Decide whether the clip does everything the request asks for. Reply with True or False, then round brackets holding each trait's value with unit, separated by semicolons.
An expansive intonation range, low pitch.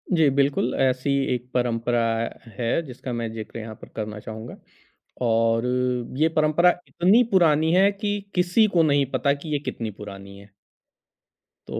True (5.8 semitones; 130 Hz)